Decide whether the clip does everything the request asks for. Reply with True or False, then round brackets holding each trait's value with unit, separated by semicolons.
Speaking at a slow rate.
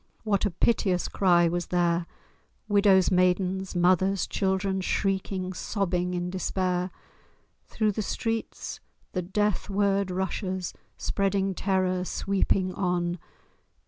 True (110 wpm)